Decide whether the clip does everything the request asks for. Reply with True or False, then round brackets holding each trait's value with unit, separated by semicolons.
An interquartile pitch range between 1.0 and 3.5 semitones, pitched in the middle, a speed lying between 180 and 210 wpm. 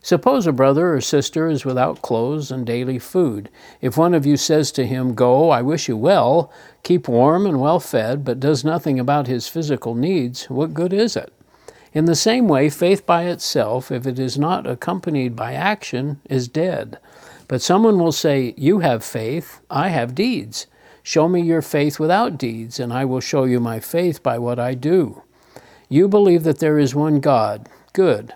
False (4.8 semitones; 145 Hz; 190 wpm)